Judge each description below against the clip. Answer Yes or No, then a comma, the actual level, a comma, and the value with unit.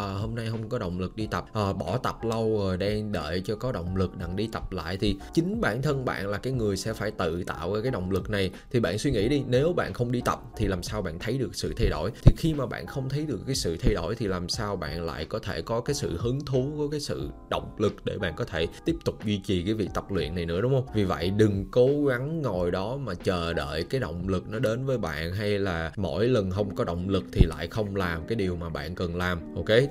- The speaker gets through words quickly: Yes, fast, 280 wpm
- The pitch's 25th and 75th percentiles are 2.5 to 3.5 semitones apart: No, average, 5.2 semitones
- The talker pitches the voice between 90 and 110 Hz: Yes, low, 105 Hz